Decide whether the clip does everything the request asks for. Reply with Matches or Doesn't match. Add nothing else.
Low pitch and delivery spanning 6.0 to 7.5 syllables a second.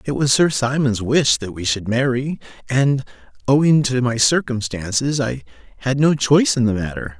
Doesn't match